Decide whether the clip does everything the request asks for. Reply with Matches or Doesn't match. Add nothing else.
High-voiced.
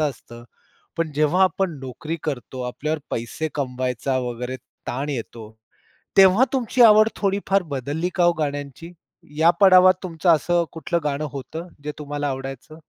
Doesn't match